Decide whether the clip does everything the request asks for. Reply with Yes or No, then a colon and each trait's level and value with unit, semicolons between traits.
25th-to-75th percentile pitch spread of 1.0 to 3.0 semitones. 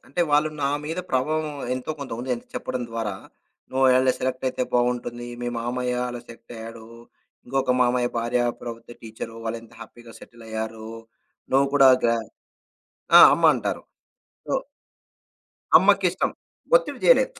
Yes: narrow, 2.5 semitones